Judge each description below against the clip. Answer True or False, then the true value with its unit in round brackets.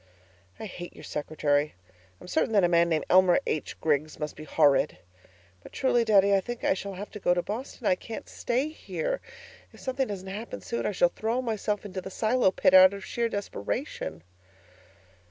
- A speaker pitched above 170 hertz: True (190 Hz)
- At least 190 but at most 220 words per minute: True (195 wpm)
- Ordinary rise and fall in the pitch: False (5.7 semitones)